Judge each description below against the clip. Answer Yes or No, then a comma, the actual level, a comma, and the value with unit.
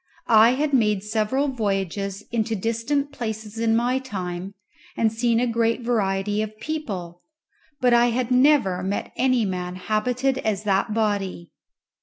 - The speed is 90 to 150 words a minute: Yes, average, 145 wpm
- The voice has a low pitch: No, high, 220 Hz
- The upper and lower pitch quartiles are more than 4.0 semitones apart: No, average, 3.7 semitones